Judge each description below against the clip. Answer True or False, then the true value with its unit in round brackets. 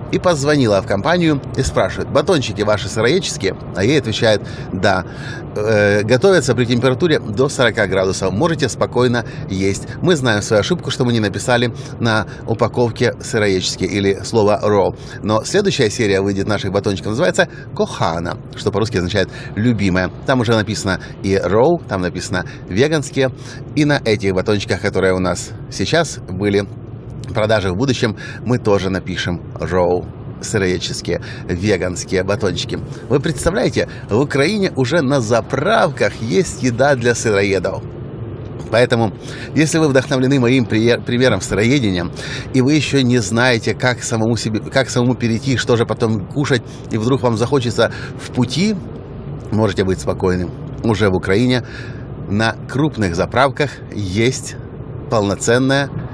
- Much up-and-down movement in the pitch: False (4.5 semitones)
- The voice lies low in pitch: True (120 Hz)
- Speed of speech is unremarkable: True (135 wpm)